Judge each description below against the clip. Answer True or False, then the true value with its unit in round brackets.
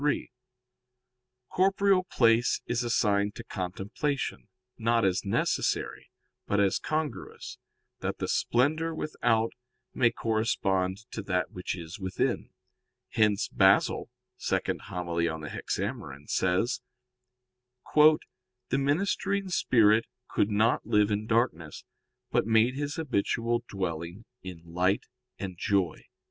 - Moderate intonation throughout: True (5.0 semitones)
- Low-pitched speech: True (110 Hz)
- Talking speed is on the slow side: True (110 wpm)